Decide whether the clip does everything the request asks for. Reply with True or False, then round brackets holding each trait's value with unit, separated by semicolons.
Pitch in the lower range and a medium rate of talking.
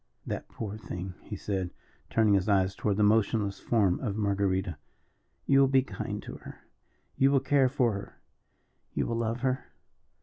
True (105 Hz; 170 wpm)